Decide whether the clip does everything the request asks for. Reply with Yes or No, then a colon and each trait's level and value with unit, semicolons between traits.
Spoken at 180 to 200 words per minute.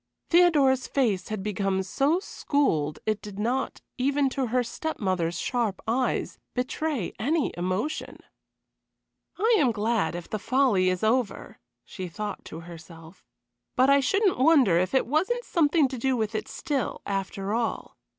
No: average, 150 wpm